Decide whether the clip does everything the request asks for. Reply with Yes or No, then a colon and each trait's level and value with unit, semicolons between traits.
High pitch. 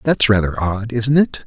No: low, 115 Hz